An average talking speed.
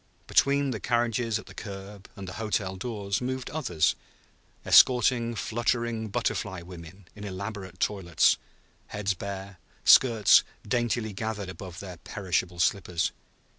No: slow, 125 wpm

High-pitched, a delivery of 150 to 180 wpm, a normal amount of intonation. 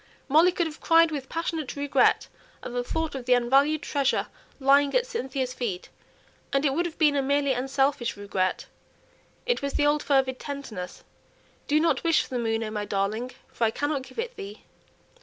No: very high, 275 Hz; average, 190 wpm; average, 3.8 semitones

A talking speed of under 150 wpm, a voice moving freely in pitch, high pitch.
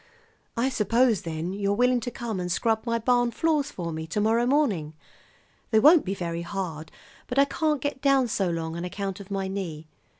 No: average, 200 wpm; wide, 5.9 semitones; high, 210 Hz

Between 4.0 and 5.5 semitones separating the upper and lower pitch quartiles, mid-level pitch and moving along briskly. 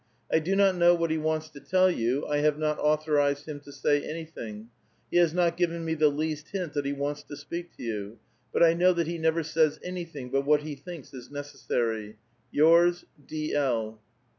No: average, 2.8 semitones; medium, 155 Hz; fast, 210 wpm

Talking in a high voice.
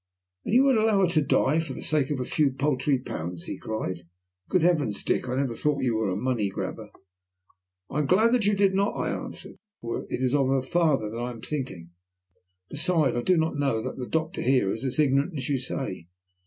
No: low, 135 Hz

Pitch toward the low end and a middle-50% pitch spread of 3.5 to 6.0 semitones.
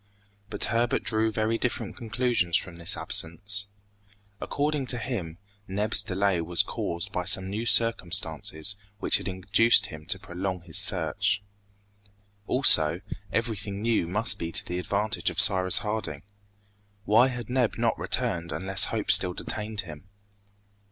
Yes: low, 100 Hz; average, 4.2 semitones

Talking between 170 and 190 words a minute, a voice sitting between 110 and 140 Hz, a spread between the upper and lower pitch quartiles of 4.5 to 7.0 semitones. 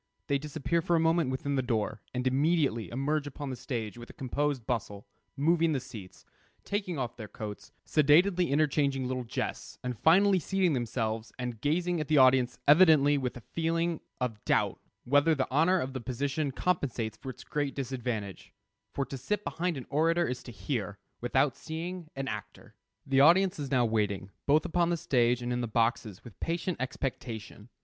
Yes: average, 180 wpm; low, 135 Hz; average, 4.8 semitones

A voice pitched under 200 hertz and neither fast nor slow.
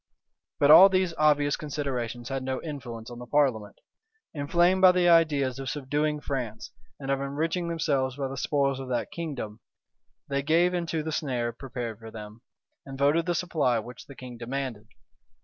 Yes: medium, 140 Hz; average, 170 wpm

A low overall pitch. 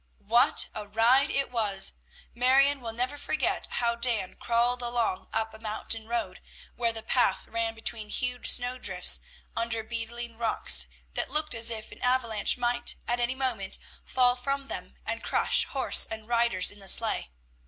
No: high, 235 Hz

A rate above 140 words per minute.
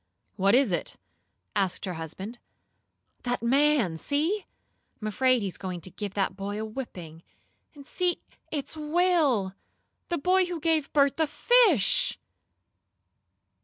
No: slow, 135 wpm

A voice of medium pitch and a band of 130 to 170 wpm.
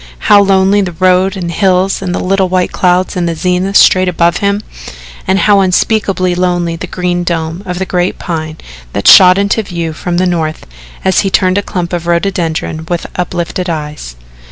No: medium, 180 Hz; average, 185 wpm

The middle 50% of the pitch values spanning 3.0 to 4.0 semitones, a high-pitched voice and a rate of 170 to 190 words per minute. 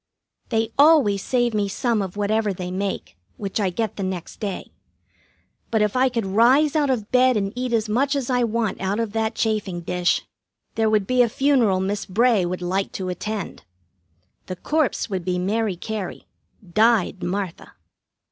Yes: average, 3.7 semitones; high, 215 Hz; average, 175 wpm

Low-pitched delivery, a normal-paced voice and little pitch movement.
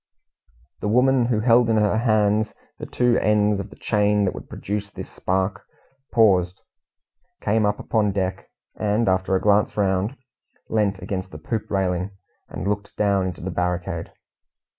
Yes: low, 105 Hz; average, 160 wpm; narrow, 2.3 semitones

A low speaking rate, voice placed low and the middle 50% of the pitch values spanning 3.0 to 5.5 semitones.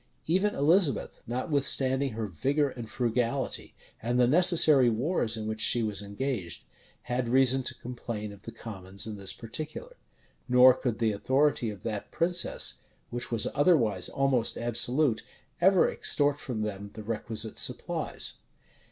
No: average, 145 wpm; low, 120 Hz; average, 4.3 semitones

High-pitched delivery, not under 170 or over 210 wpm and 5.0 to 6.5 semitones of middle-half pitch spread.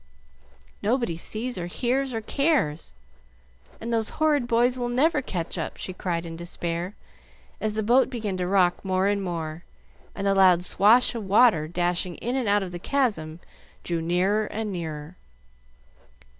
No: high, 200 Hz; average, 160 wpm; wide, 5.4 semitones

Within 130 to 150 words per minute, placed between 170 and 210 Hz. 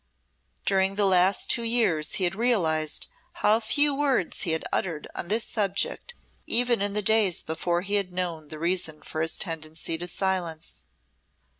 No: average, 165 wpm; medium, 185 Hz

